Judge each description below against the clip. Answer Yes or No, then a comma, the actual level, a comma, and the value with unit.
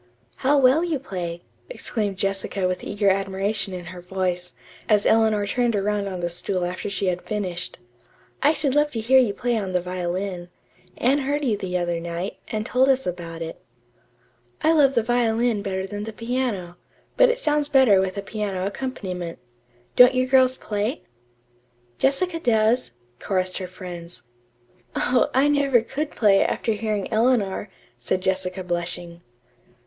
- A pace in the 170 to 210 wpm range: No, average, 160 wpm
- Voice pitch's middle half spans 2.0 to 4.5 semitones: No, wide, 5.5 semitones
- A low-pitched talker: No, high, 205 Hz